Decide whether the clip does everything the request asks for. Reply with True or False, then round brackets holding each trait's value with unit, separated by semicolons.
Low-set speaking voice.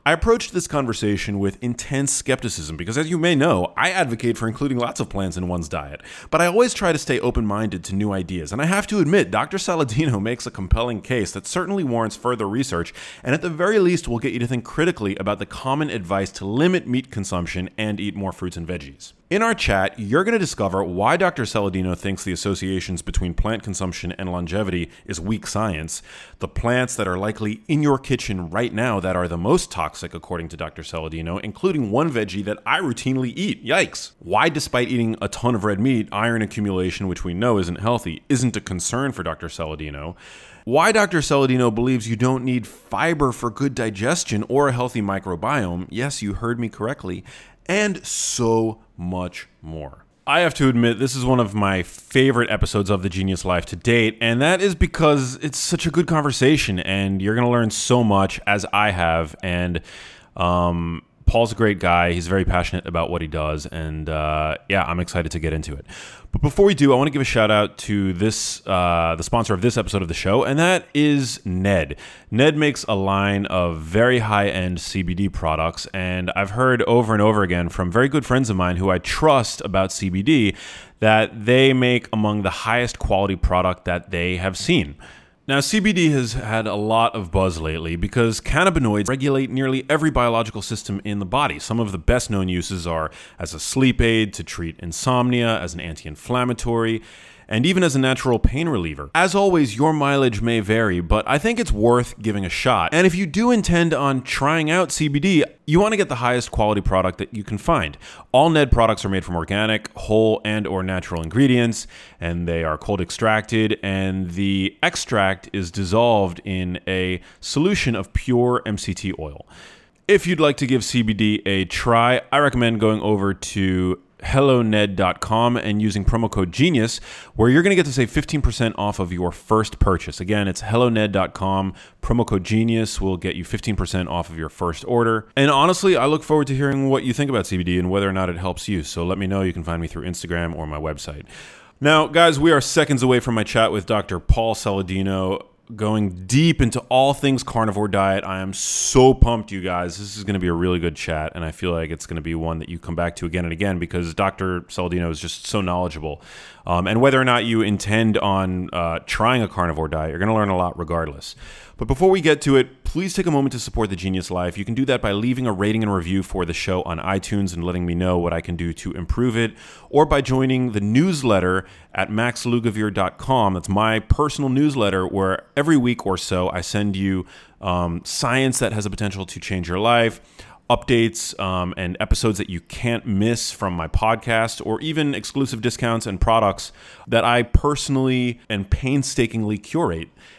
True (105 Hz)